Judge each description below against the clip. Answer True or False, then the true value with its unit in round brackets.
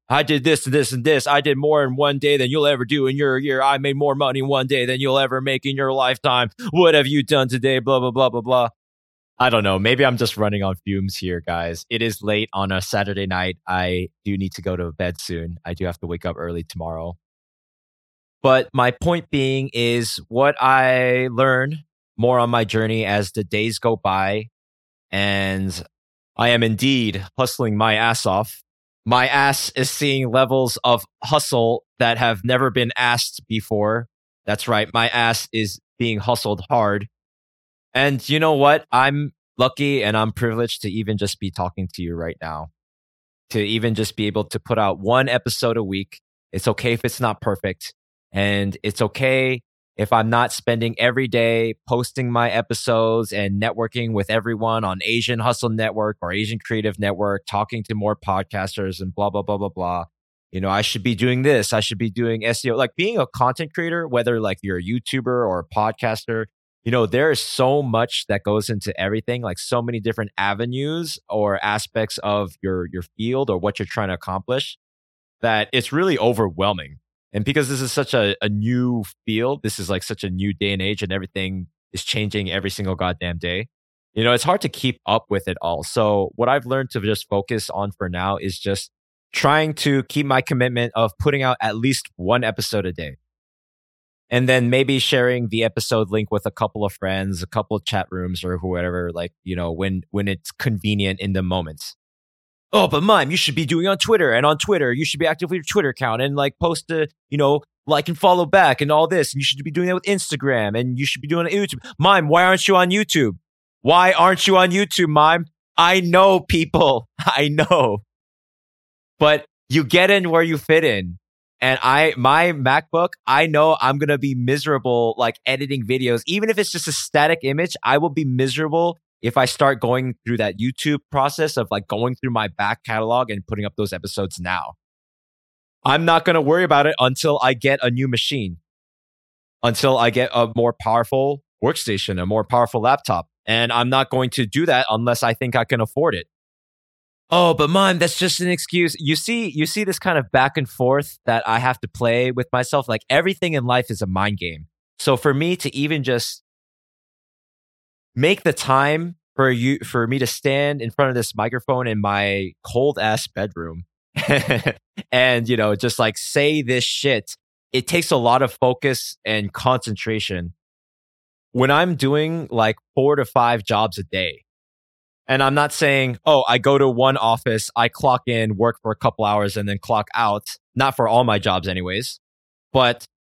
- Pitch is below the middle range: True (120 Hz)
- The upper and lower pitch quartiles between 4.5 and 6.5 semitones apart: True (5.2 semitones)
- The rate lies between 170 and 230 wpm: True (200 wpm)